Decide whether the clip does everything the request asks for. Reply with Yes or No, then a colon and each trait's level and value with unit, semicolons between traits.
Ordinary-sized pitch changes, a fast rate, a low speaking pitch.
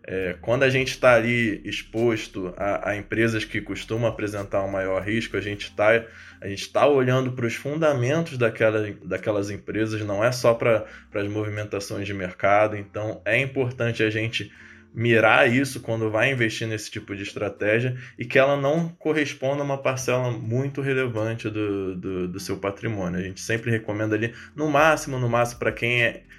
No: average, 3.5 semitones; average, 175 wpm; low, 110 Hz